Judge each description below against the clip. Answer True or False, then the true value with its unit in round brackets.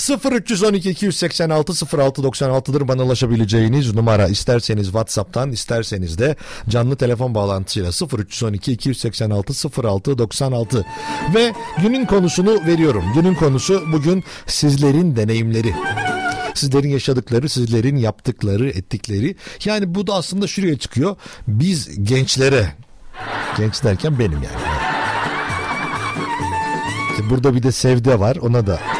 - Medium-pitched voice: False (130 Hz)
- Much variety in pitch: True (6.4 semitones)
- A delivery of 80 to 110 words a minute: True (105 wpm)